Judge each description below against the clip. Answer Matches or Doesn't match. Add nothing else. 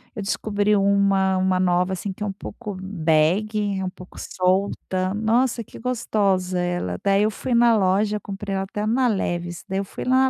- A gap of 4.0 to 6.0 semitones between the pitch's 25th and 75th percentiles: Doesn't match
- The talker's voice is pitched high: Matches